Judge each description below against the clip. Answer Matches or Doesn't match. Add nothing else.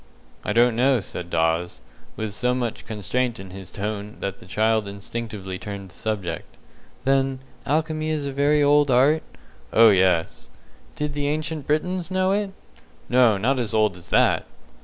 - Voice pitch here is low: Matches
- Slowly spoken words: Doesn't match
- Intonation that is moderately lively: Doesn't match